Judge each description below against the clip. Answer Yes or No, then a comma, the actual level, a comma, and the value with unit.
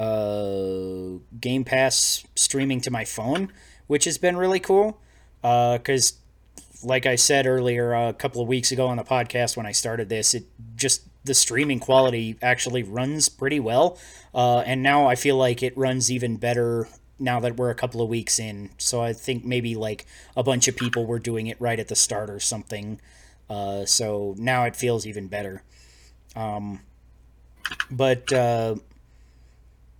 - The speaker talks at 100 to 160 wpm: No, average, 170 wpm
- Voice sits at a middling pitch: No, low, 120 Hz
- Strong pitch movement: No, average, 3.4 semitones